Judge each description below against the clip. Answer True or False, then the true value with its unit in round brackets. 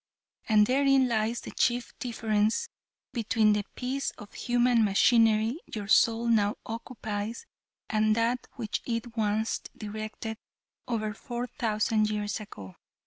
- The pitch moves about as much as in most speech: False (2.1 semitones)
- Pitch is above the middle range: True (225 Hz)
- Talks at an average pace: False (125 wpm)